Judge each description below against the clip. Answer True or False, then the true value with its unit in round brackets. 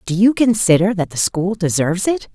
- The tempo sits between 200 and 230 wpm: True (205 wpm)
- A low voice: False (190 Hz)